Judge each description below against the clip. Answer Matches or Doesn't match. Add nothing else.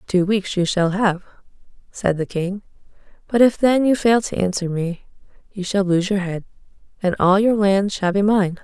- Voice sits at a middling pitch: Doesn't match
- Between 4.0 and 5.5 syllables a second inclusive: Matches